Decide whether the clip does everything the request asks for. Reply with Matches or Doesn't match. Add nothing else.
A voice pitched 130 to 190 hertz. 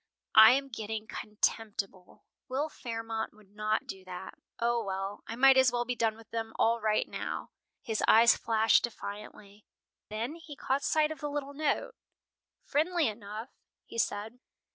Doesn't match